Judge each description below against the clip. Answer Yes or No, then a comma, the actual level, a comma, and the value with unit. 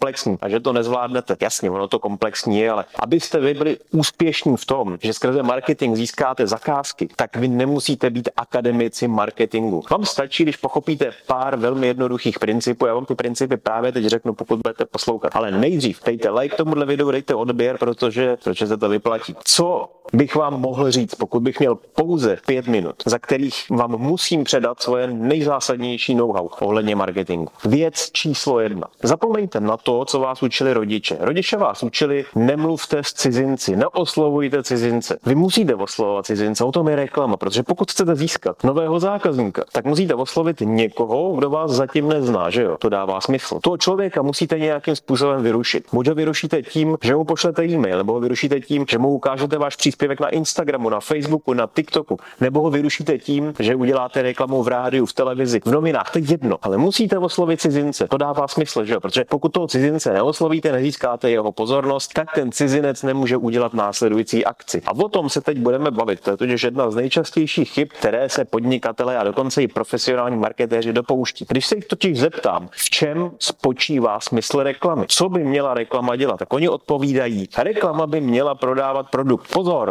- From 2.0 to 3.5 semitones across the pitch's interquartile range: No, average, 4.1 semitones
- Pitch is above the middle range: No, low, 135 Hz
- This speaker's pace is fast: Yes, fast, 180 wpm